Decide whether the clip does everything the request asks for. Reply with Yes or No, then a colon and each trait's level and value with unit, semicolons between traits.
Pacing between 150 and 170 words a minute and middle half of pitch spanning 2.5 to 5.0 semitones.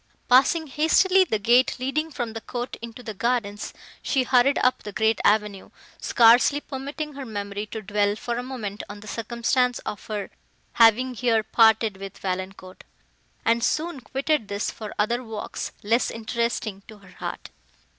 Yes: average, 160 wpm; average, 3.4 semitones